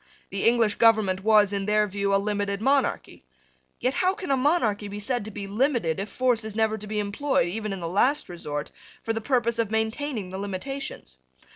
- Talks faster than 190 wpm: Yes, average, 200 wpm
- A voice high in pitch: Yes, high, 215 Hz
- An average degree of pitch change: Yes, average, 3.4 semitones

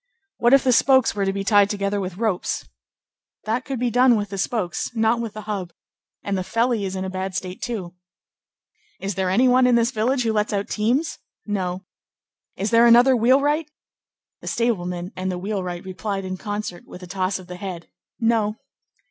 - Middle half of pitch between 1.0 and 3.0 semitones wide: No, average, 3.9 semitones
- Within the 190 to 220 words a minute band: Yes, average, 195 wpm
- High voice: Yes, high, 205 Hz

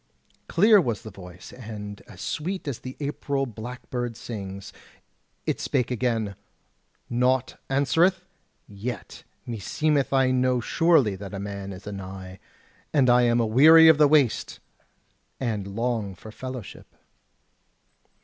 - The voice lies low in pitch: Yes, low, 120 Hz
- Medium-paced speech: No, slow, 125 wpm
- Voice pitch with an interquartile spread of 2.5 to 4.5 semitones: No, average, 4.9 semitones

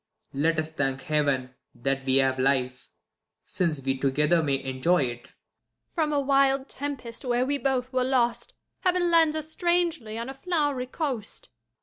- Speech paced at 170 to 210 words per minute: No, average, 160 wpm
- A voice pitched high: Yes, high, 230 Hz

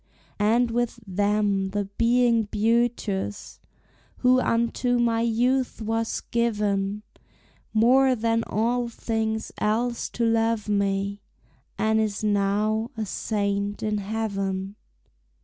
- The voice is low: No, high, 220 Hz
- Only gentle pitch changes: Yes, narrow, 2.3 semitones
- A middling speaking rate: No, slow, 105 wpm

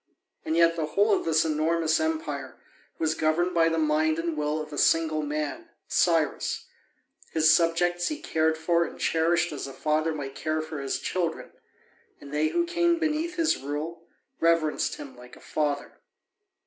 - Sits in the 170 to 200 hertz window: No, medium, 160 Hz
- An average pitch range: No, narrow, 1.9 semitones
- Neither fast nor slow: Yes, average, 170 wpm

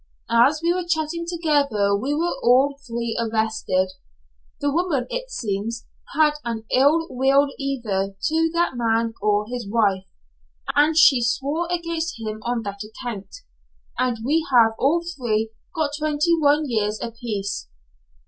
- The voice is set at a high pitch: Yes, very high, 250 Hz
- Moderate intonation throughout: No, wide, 5.9 semitones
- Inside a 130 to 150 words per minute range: Yes, average, 145 wpm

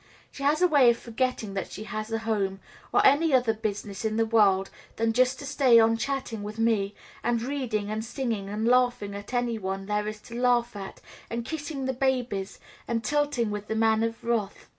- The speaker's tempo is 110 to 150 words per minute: No, fast, 205 wpm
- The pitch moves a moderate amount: Yes, average, 3.2 semitones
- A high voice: Yes, high, 225 Hz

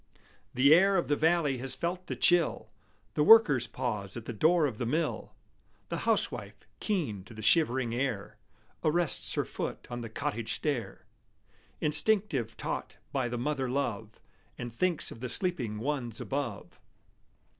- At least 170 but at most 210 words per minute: No, average, 155 wpm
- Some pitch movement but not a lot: No, wide, 5.7 semitones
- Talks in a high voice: No, low, 135 Hz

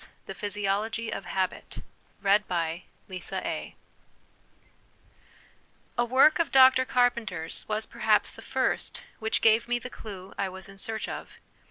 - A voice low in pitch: No, high, 215 Hz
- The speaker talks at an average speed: No, slow, 120 wpm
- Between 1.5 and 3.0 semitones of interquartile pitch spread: No, average, 4.0 semitones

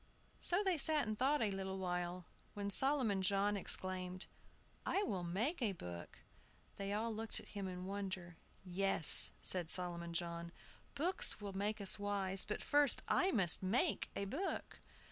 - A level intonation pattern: No, average, 3.5 semitones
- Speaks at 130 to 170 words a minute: Yes, average, 160 wpm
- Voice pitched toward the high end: Yes, high, 195 Hz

